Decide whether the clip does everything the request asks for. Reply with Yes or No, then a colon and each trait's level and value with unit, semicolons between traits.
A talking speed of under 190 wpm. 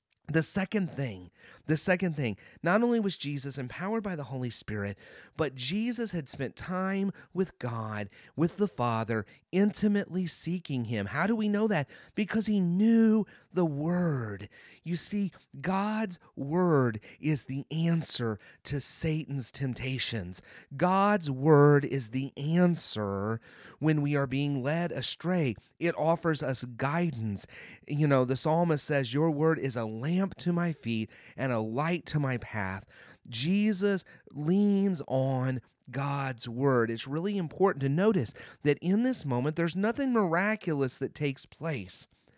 Yes: average, 145 wpm